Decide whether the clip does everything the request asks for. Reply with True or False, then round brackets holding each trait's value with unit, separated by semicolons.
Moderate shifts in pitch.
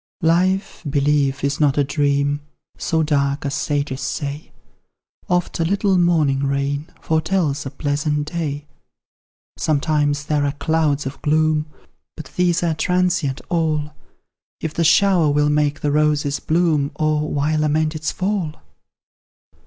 False (2.0 semitones)